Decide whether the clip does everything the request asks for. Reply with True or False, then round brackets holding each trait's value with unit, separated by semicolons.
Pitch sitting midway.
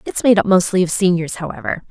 True (180 Hz)